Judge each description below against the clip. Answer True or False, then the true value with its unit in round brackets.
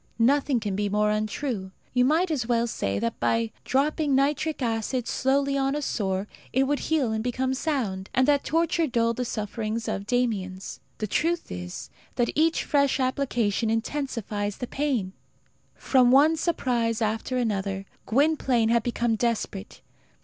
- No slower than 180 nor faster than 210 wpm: False (155 wpm)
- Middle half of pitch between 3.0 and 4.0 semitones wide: False (4.6 semitones)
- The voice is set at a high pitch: True (240 Hz)